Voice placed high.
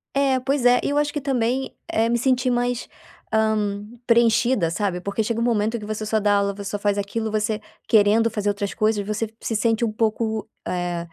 Yes: high, 220 Hz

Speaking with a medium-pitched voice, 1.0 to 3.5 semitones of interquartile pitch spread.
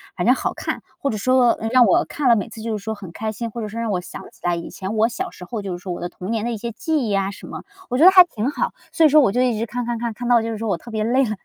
No: high, 225 Hz; average, 3.0 semitones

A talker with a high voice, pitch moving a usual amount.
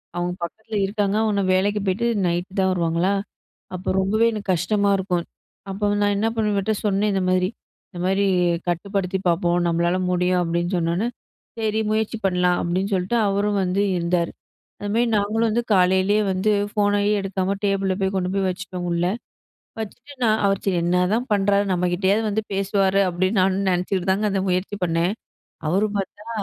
No: high, 195 Hz; narrow, 2.2 semitones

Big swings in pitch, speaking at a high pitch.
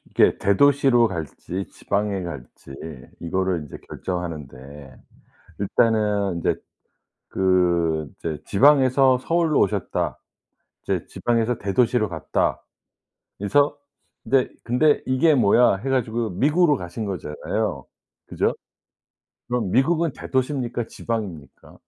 No: wide, 6.7 semitones; low, 105 Hz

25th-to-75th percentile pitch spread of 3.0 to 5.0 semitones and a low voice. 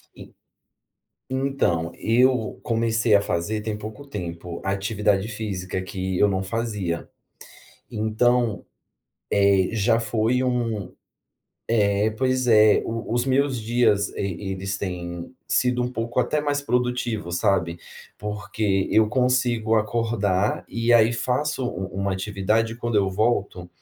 Yes: average, 3.6 semitones; low, 110 Hz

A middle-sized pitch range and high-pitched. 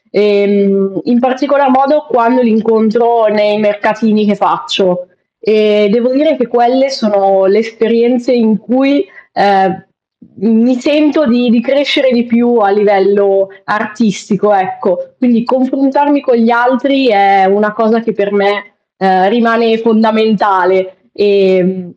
Yes: average, 3.5 semitones; high, 220 Hz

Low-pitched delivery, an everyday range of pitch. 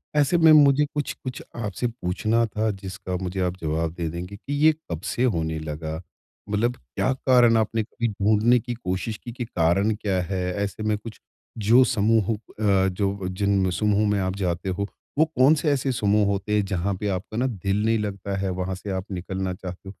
Yes: low, 100 Hz; average, 3.7 semitones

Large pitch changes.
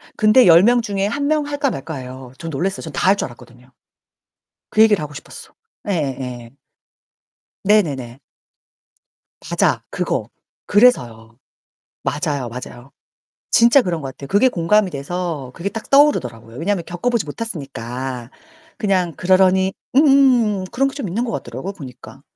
Yes: wide, 8.7 semitones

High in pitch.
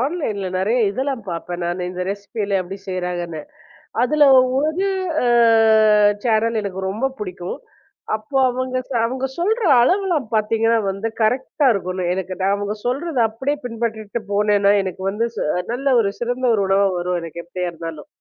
Yes: high, 215 Hz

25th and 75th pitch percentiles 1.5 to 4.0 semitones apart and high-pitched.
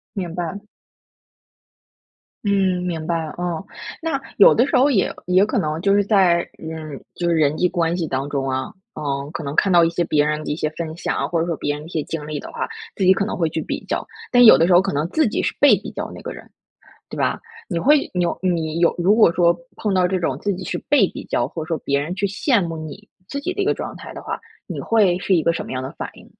No: average, 3.7 semitones; medium, 170 Hz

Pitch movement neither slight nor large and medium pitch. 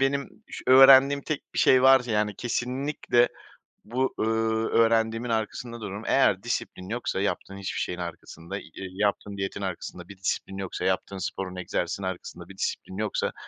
No: average, 4.2 semitones; low, 110 Hz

